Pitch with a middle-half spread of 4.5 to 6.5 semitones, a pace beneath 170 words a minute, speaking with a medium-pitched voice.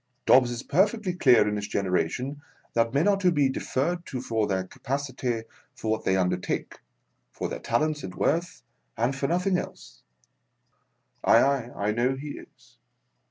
No: average, 5.2 semitones; average, 160 wpm; low, 130 Hz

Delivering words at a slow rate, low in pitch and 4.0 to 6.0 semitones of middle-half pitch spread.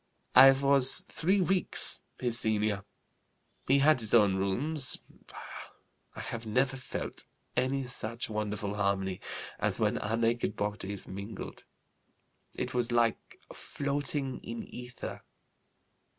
Yes: slow, 115 wpm; low, 120 Hz; average, 4.3 semitones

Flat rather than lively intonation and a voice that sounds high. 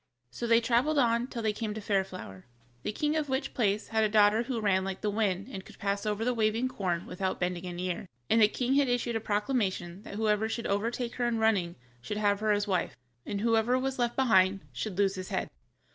No: average, 3.3 semitones; high, 215 Hz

